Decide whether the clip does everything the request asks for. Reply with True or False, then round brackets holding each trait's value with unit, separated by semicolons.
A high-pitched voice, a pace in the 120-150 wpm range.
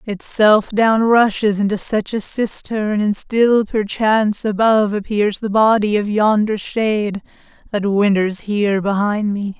True (210 Hz; 140 wpm)